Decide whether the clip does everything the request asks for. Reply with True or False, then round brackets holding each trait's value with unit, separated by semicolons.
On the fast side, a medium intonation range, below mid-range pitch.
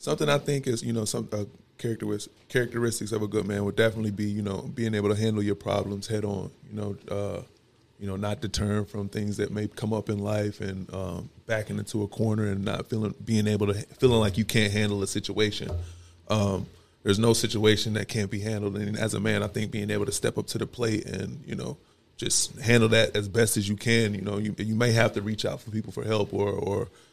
False (240 wpm; 1.5 semitones; 105 Hz)